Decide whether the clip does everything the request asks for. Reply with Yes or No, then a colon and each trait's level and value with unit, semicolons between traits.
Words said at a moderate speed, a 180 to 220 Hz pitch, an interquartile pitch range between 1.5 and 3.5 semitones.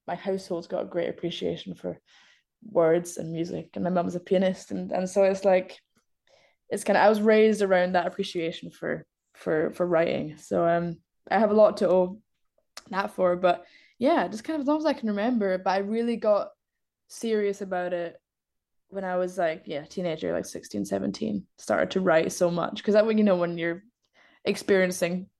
Yes: average, 195 wpm; medium, 185 Hz; average, 3.2 semitones